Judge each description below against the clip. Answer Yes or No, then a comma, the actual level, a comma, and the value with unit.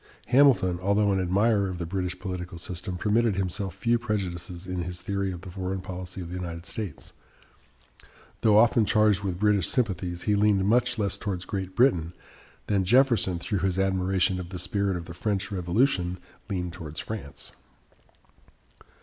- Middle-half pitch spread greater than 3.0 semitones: No, narrow, 2.6 semitones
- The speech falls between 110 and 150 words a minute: No, average, 165 wpm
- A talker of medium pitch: No, very low, 95 Hz